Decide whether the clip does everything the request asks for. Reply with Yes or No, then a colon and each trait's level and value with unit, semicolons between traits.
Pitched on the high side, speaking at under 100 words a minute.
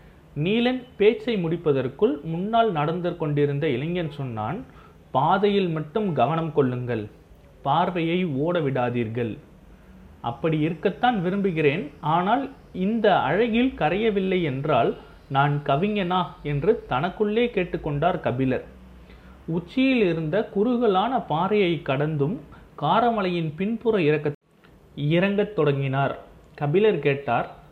No: medium, 170 Hz; average, 90 wpm